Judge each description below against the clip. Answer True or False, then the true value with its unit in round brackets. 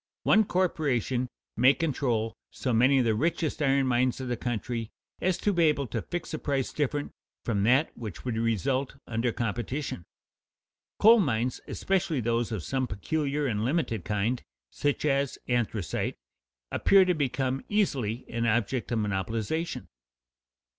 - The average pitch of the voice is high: False (130 Hz)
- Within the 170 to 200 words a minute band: False (145 wpm)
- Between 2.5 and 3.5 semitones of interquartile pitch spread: False (4.2 semitones)